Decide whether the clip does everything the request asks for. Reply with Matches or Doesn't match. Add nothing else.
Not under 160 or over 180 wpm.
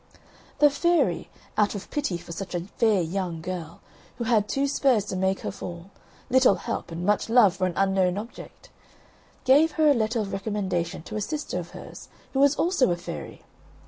Doesn't match